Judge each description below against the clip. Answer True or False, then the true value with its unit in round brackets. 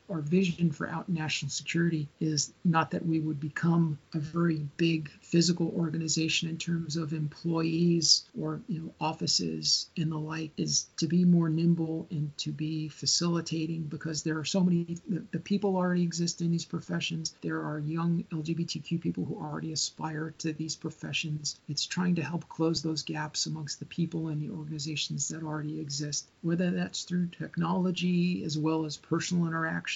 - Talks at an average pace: True (170 wpm)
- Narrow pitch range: True (1.6 semitones)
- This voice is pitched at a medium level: True (160 Hz)